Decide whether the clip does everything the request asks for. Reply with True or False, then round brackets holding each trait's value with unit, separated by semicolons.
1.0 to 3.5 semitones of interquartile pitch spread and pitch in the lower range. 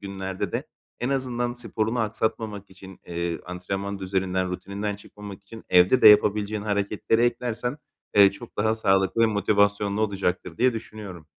True (2.6 semitones; 100 Hz)